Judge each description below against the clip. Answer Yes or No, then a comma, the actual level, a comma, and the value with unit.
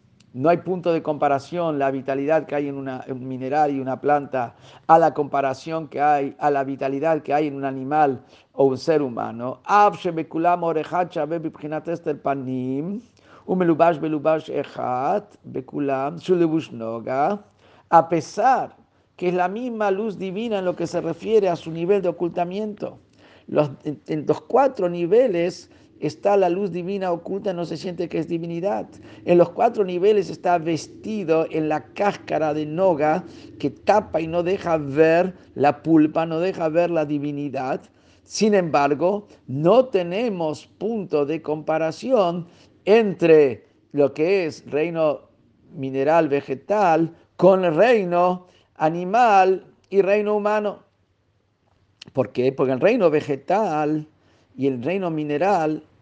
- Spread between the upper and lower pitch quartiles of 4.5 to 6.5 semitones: No, average, 4.1 semitones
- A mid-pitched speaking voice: Yes, medium, 160 Hz